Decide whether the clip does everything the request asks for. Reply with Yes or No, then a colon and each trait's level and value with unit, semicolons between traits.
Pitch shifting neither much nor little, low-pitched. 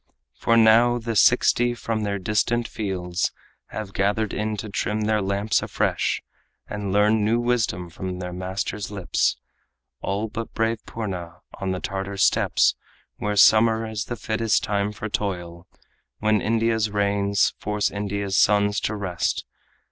No: narrow, 2.2 semitones; low, 105 Hz